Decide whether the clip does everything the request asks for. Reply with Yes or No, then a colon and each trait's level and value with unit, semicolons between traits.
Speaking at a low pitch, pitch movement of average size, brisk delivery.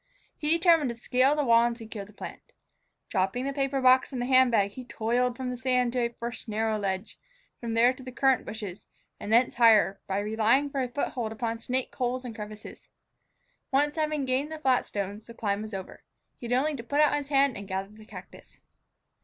No: high, 245 Hz; average, 3.4 semitones; fast, 215 wpm